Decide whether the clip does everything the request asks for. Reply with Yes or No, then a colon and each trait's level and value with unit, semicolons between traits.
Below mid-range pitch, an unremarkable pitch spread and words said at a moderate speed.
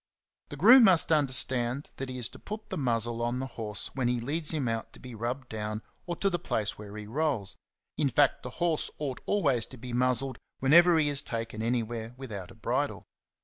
No: low, 125 Hz; average, 4.3 semitones; fast, 220 wpm